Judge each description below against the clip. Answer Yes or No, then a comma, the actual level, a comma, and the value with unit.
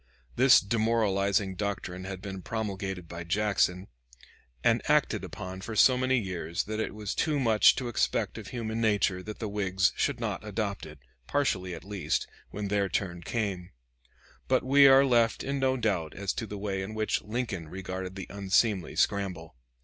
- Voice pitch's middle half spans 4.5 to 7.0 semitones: No, average, 3.2 semitones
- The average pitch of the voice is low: Yes, low, 100 Hz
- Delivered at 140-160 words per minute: No, average, 170 wpm